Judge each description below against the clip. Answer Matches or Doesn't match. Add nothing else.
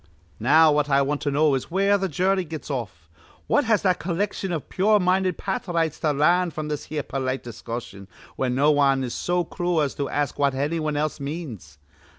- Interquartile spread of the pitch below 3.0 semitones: Doesn't match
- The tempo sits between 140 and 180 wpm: Doesn't match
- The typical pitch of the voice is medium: Matches